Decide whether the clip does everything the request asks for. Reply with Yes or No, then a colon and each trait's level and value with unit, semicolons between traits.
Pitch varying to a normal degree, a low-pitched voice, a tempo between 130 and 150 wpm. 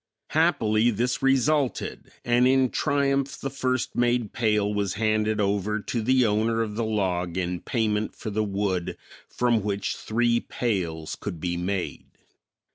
Yes: average, 3.5 semitones; low, 110 Hz; average, 145 wpm